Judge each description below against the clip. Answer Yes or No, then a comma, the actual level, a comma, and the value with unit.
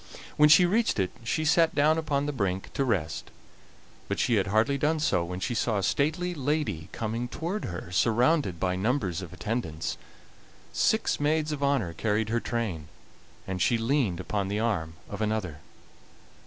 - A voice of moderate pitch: No, low, 115 Hz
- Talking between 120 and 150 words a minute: No, average, 170 wpm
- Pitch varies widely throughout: Yes, wide, 7.8 semitones